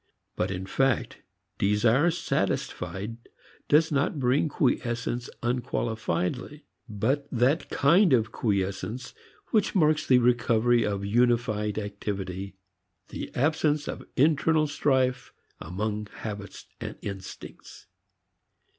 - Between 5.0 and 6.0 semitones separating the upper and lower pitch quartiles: Yes, wide, 5.5 semitones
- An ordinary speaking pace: No, slow, 100 wpm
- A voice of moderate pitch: No, low, 120 Hz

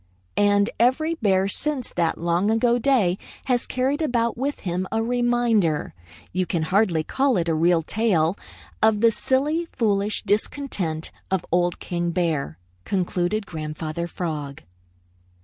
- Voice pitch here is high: Yes, high, 200 Hz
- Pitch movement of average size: No, wide, 5.9 semitones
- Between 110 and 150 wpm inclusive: Yes, average, 140 wpm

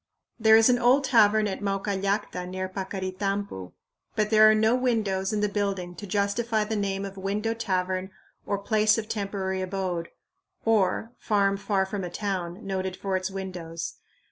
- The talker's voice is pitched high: Yes, high, 200 Hz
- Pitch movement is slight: Yes, narrow, 2.3 semitones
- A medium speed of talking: Yes, average, 165 wpm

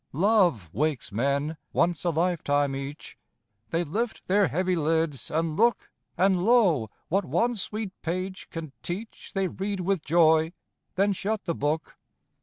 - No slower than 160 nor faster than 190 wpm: No, average, 145 wpm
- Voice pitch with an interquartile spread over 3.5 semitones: Yes, average, 4.1 semitones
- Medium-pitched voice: Yes, medium, 170 Hz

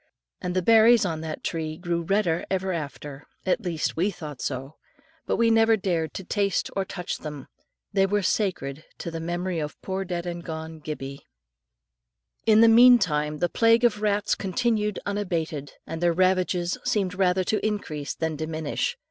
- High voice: No, medium, 180 Hz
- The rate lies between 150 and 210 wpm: Yes, average, 170 wpm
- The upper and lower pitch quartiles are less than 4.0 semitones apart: No, average, 4.3 semitones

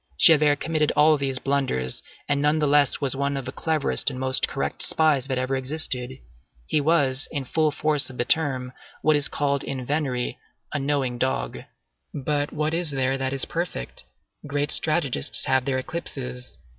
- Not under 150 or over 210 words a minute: Yes, average, 170 wpm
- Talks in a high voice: No, medium, 140 Hz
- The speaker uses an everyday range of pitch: No, narrow, 2.3 semitones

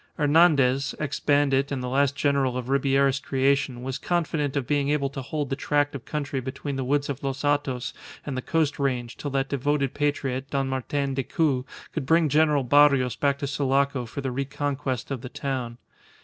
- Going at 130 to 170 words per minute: No, average, 190 wpm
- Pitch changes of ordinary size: No, narrow, 1.6 semitones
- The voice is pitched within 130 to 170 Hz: Yes, medium, 140 Hz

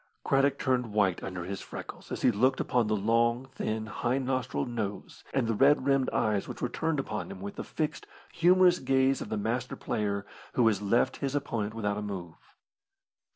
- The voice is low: Yes, low, 120 Hz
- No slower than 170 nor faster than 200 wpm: Yes, average, 195 wpm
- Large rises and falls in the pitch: No, average, 4.5 semitones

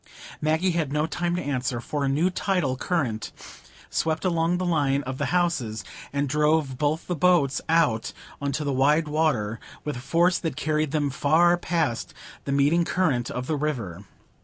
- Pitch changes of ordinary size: Yes, average, 3.7 semitones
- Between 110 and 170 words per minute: No, average, 180 wpm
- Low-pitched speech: No, medium, 150 Hz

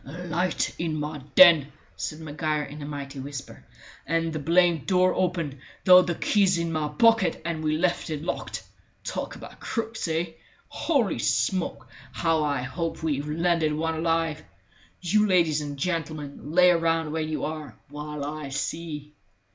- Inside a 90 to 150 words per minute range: No, average, 160 wpm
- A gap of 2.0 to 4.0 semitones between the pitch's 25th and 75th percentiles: Yes, narrow, 2.6 semitones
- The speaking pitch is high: No, medium, 160 Hz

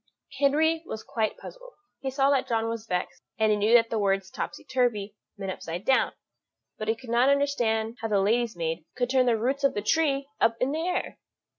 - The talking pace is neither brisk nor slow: No, fast, 210 wpm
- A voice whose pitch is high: Yes, high, 230 Hz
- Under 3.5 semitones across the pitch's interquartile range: No, average, 4.2 semitones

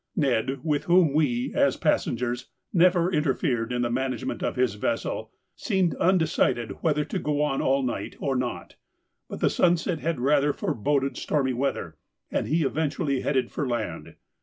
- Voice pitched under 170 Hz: Yes, medium, 140 Hz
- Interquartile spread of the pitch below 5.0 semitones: Yes, average, 4.2 semitones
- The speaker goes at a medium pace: Yes, average, 160 wpm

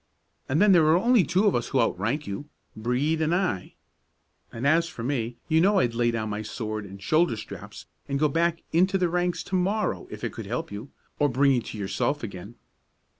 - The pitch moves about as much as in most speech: No, wide, 7.2 semitones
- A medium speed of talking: No, fast, 220 wpm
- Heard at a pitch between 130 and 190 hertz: Yes, medium, 140 Hz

